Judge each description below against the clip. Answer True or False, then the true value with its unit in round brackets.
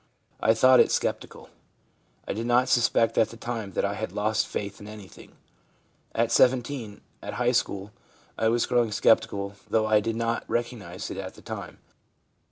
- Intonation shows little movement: True (2.3 semitones)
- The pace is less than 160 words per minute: False (175 wpm)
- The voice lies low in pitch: True (115 Hz)